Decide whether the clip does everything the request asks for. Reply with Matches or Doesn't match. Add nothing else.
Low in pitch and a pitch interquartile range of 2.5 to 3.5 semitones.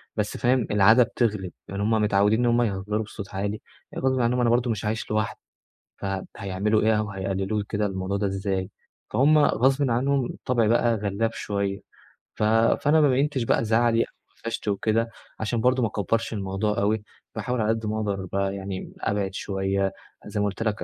Matches